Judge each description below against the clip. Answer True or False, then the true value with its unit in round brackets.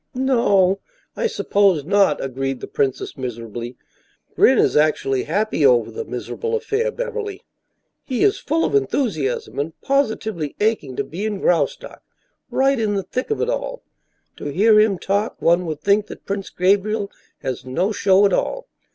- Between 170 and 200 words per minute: False (160 wpm)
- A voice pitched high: True (200 Hz)